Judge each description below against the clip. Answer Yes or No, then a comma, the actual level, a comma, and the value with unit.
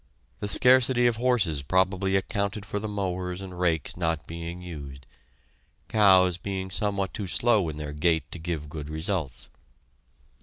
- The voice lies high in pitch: No, very low, 90 Hz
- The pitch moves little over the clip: No, average, 3.9 semitones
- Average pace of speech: Yes, average, 150 wpm